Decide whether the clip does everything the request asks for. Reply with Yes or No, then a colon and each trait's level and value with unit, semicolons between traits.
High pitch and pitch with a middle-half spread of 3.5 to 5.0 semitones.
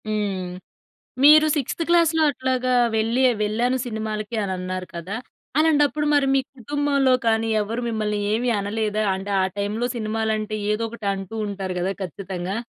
Yes: high, 220 Hz; average, 4.1 semitones